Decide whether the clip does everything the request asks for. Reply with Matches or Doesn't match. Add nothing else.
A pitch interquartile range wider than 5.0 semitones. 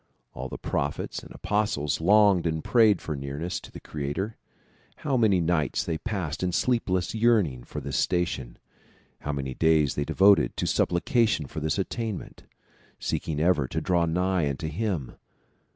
Matches